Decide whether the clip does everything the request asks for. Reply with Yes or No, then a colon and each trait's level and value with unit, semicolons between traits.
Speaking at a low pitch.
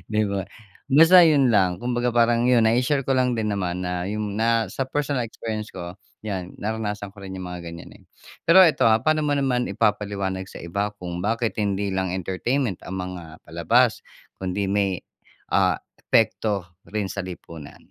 Yes: low, 105 Hz